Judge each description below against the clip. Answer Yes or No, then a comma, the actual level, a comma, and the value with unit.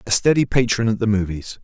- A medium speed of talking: No, fast, 220 wpm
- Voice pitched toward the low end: Yes, low, 110 Hz